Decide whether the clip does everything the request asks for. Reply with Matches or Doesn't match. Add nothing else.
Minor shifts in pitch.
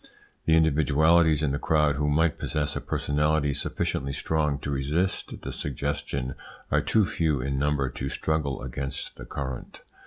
Matches